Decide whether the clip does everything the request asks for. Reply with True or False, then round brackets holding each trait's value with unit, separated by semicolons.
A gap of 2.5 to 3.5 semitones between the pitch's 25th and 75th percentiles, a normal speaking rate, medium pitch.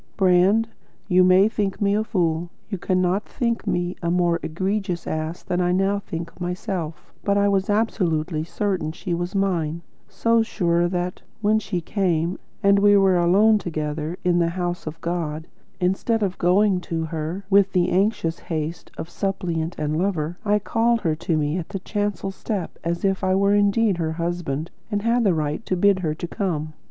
True (3.0 semitones; 180 wpm; 180 Hz)